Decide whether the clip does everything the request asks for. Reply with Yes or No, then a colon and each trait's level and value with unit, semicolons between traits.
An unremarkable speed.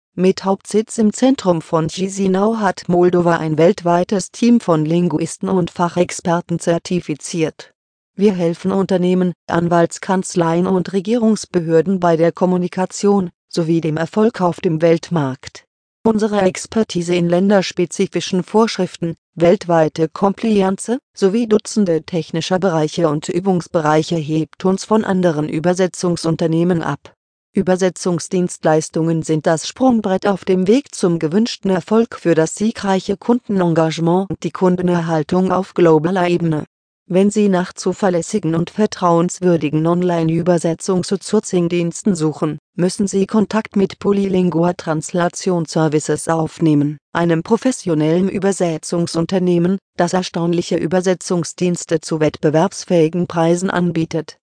No: slow, 110 wpm